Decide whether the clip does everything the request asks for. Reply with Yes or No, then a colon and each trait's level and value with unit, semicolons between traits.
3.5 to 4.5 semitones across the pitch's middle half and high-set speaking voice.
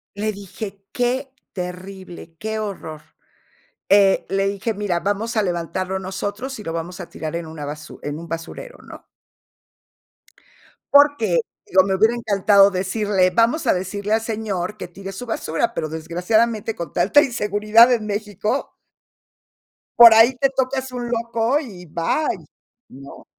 Yes: average, 4.1 semitones; high, 200 Hz